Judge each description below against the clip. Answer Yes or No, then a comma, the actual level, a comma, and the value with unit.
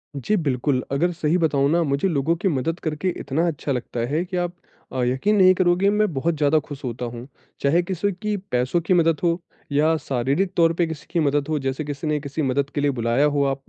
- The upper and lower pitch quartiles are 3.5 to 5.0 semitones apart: Yes, average, 3.9 semitones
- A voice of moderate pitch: Yes, medium, 150 Hz